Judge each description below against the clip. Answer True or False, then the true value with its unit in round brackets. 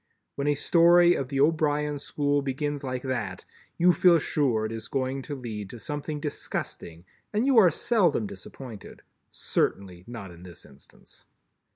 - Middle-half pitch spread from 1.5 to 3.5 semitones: False (5.4 semitones)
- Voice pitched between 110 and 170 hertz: True (140 Hz)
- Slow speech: False (160 wpm)